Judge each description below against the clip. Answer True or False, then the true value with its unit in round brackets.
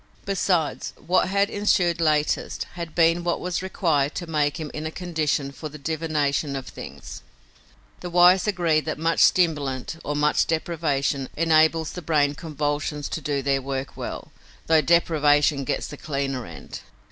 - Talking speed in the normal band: True (160 wpm)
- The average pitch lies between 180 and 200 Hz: False (155 Hz)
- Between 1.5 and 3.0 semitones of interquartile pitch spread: True (2.7 semitones)